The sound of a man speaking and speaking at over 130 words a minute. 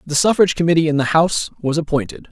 Yes: male; fast, 205 wpm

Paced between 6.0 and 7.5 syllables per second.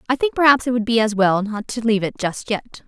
Yes: 6.1 syllables/s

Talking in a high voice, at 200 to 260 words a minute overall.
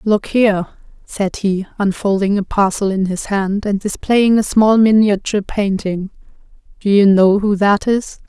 No: high, 205 Hz; average, 160 wpm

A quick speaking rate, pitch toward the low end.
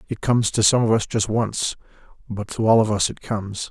Yes: fast, 245 wpm; low, 110 Hz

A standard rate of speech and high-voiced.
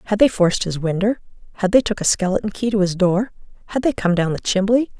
No: fast, 215 wpm; high, 200 Hz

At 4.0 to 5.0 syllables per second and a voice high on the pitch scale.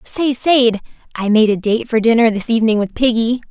No: 5.3 syllables/s; high, 230 Hz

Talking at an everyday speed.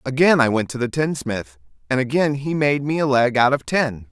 No: fast, 235 wpm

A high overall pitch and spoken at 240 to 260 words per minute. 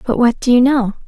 No: high, 245 Hz; fast, 280 wpm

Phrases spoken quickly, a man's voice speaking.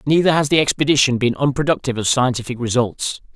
No: average, 160 wpm; male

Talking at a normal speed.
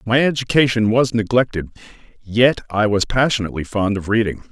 Yes: average, 145 wpm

